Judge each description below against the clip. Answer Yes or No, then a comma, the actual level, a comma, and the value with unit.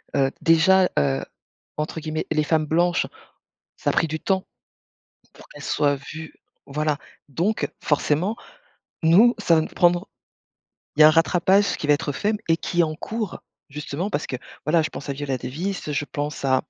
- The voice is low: No, medium, 155 Hz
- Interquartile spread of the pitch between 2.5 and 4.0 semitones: Yes, average, 3.1 semitones